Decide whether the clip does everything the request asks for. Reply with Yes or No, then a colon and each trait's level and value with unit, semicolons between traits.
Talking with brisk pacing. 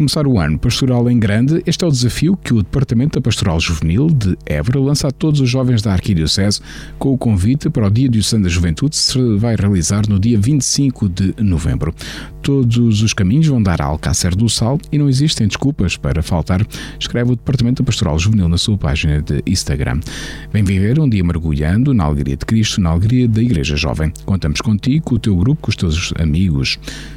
Yes: fast, 205 wpm